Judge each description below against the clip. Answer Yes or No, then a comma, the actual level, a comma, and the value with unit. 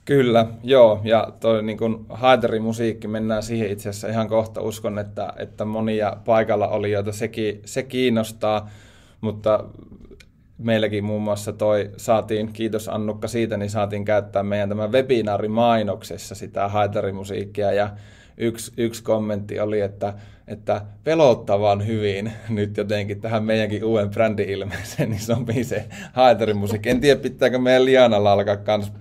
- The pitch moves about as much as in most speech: No, narrow, 1.8 semitones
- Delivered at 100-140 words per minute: Yes, average, 135 wpm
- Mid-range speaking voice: No, low, 110 Hz